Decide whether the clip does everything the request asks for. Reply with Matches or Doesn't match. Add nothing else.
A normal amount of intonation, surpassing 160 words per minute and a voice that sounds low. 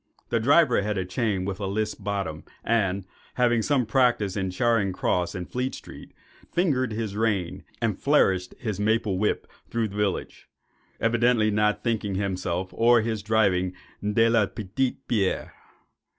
Doesn't match